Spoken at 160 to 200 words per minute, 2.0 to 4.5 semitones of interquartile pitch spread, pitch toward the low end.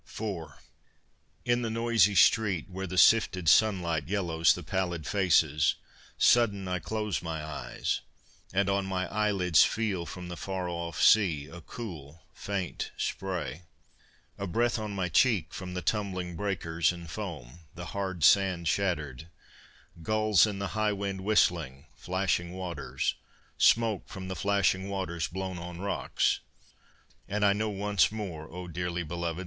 No: average, 145 wpm; average, 3.1 semitones; very low, 95 Hz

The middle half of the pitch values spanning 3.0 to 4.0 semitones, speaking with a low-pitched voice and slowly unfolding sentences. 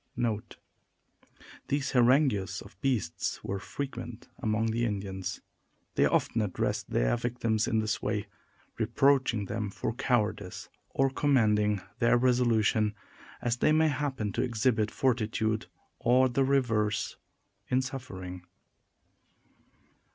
Yes: average, 3.5 semitones; low, 115 Hz; slow, 115 wpm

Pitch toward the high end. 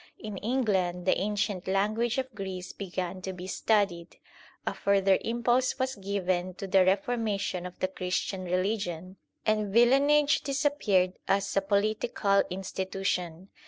Yes: high, 195 Hz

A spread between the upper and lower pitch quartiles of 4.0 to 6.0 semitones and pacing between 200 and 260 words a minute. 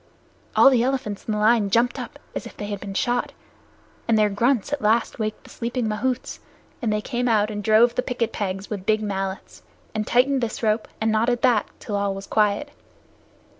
No: average, 2.7 semitones; fast, 205 wpm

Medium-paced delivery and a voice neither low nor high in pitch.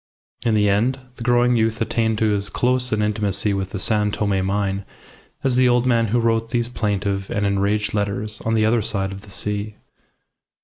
No: average, 195 wpm; low, 105 Hz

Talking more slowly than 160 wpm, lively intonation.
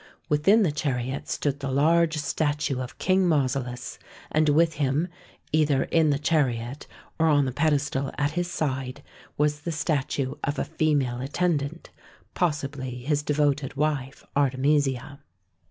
No: average, 140 wpm; narrow, 2.4 semitones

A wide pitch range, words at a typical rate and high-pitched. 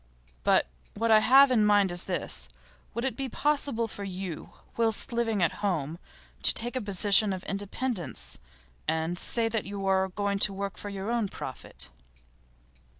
No: average, 3.4 semitones; average, 165 wpm; high, 205 Hz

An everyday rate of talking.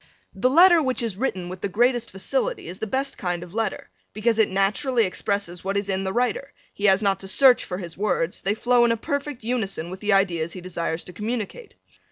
No: fast, 225 wpm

